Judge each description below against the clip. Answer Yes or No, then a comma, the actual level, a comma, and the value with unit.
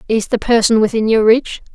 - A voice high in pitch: Yes, high, 220 Hz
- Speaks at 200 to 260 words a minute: Yes, fast, 205 wpm